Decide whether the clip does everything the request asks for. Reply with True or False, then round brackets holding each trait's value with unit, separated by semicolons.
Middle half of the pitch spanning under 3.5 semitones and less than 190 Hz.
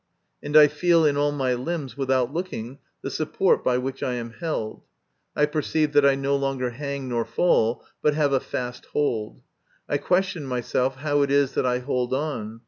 True (2.8 semitones; 140 Hz)